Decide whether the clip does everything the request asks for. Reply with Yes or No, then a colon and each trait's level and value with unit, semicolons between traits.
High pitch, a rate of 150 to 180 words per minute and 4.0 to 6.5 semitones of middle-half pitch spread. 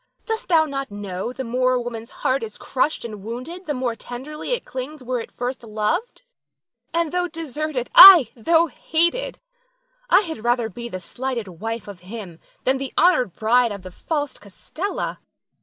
Yes: very high, 255 Hz; average, 175 wpm; wide, 5.6 semitones